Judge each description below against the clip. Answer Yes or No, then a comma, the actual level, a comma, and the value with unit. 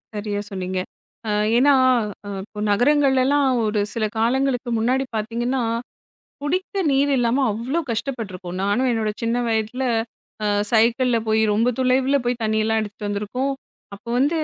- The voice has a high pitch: Yes, high, 235 Hz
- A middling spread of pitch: Yes, average, 3.6 semitones